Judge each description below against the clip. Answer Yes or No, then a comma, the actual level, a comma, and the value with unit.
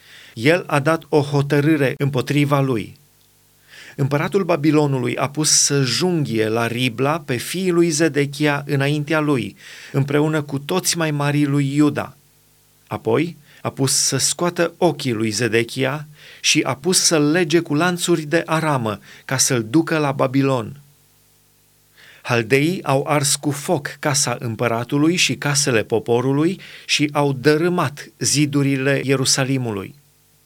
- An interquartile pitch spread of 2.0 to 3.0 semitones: Yes, narrow, 2.6 semitones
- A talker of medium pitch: Yes, medium, 145 Hz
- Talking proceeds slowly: No, average, 130 wpm